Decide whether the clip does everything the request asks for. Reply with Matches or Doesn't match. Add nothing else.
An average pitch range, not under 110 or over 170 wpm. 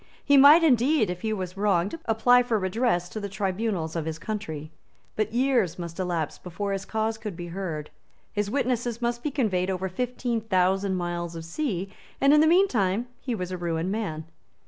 Doesn't match